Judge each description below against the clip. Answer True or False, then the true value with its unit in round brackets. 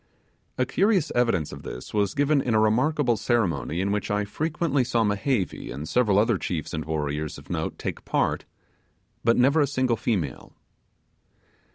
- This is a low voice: True (110 Hz)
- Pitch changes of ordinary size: False (5.9 semitones)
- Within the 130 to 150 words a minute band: False (165 wpm)